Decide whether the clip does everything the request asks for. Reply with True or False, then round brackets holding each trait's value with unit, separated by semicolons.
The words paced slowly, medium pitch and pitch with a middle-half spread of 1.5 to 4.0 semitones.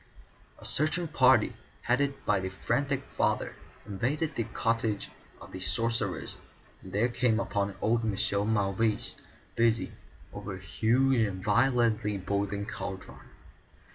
False (125 wpm; 115 Hz; 3.5 semitones)